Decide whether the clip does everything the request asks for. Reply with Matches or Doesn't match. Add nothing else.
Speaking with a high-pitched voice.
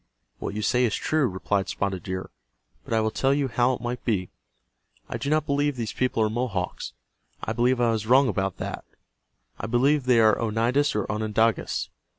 Doesn't match